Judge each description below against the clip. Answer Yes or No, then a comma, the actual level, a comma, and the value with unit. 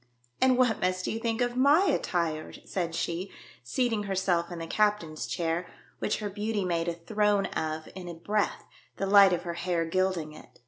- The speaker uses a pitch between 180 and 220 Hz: Yes, medium, 185 Hz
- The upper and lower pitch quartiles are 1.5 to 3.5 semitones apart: No, average, 3.9 semitones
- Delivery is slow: No, average, 195 wpm